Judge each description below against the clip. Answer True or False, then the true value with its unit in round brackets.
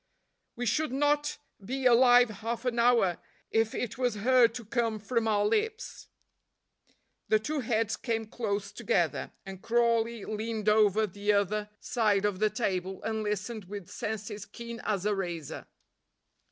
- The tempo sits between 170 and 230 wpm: False (150 wpm)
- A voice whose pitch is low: False (220 Hz)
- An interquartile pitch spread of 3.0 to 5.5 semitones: False (2.5 semitones)